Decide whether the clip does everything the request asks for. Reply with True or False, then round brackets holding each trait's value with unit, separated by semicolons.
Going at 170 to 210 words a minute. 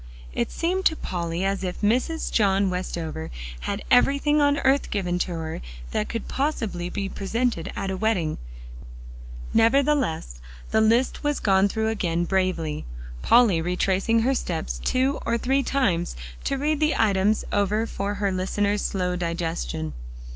False (145 wpm)